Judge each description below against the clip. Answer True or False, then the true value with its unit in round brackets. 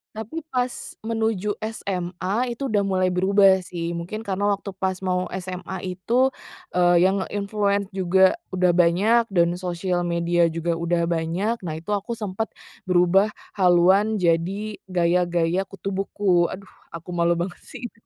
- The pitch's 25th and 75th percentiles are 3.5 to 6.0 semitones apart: False (2.7 semitones)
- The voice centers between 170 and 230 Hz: True (185 Hz)